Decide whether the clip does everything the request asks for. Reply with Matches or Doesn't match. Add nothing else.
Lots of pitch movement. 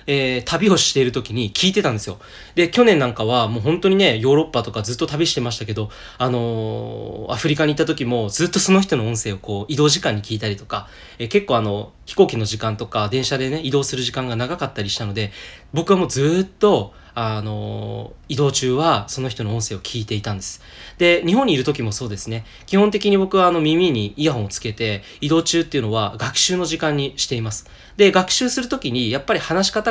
Matches